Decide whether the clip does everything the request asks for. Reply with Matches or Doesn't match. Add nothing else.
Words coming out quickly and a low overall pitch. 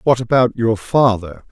Doesn't match